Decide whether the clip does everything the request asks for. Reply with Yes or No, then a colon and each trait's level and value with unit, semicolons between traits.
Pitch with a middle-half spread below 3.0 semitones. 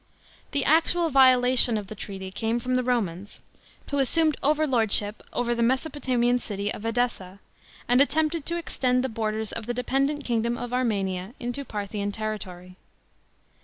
No: average, 3.9 semitones